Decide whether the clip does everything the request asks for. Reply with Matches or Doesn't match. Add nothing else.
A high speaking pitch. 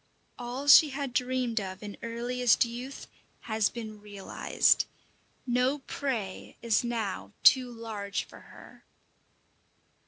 Matches